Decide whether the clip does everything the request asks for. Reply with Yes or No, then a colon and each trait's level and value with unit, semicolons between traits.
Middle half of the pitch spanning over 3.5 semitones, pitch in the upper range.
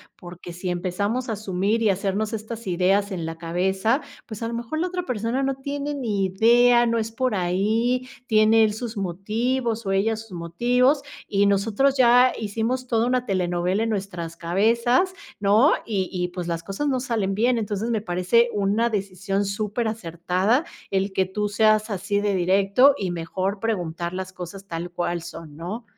Yes: average, 3.9 semitones; high, 205 Hz